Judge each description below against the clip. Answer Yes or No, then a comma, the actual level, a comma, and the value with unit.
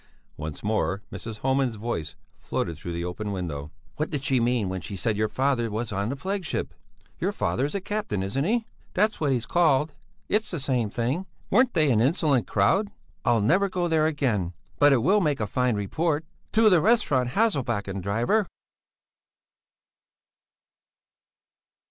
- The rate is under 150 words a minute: No, average, 165 wpm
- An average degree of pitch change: No, wide, 7.8 semitones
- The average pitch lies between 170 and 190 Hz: No, low, 125 Hz